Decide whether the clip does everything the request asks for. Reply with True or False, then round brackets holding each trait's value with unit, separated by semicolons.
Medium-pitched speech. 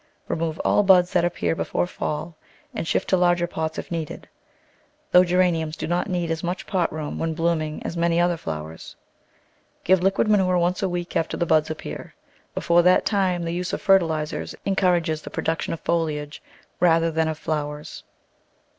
True (170 Hz)